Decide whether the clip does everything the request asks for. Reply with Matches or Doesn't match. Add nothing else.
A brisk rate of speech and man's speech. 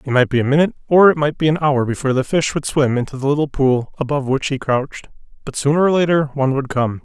Matches